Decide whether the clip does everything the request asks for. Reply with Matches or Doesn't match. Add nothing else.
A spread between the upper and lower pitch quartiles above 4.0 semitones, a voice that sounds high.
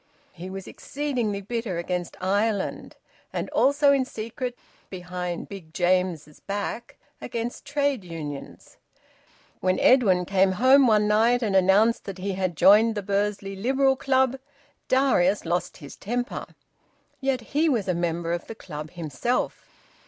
Matches